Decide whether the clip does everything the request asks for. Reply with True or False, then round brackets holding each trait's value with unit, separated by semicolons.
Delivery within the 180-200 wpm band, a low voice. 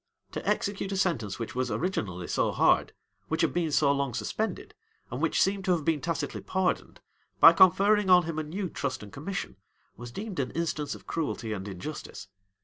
False (190 wpm; 160 Hz)